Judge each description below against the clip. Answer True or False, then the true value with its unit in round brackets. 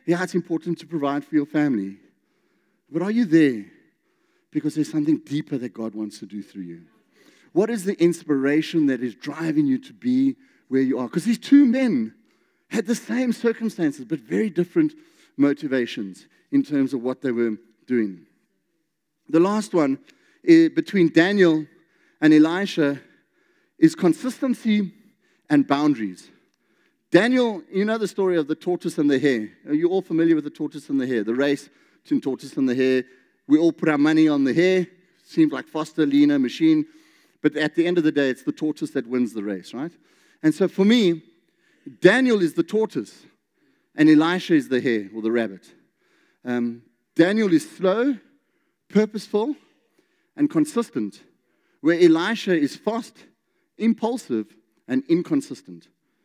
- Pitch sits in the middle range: True (175 Hz)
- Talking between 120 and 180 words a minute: True (160 wpm)